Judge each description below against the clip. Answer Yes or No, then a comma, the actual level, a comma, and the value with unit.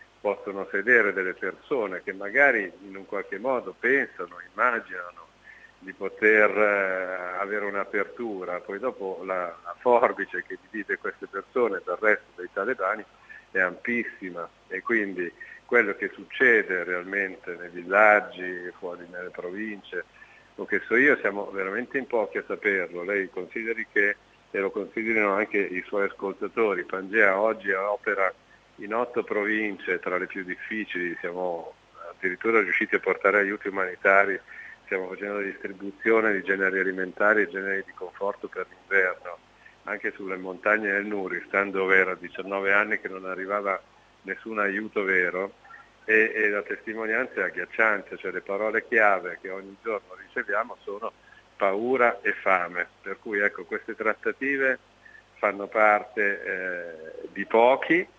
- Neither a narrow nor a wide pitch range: Yes, average, 3.1 semitones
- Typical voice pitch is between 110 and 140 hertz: No, low, 100 Hz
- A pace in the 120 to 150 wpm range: Yes, average, 140 wpm